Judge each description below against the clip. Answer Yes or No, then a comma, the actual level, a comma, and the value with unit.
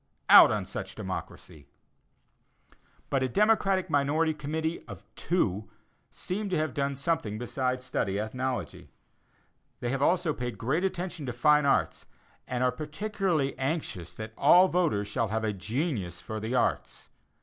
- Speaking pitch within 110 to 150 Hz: Yes, low, 135 Hz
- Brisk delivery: No, average, 145 wpm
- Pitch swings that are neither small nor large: No, wide, 6.6 semitones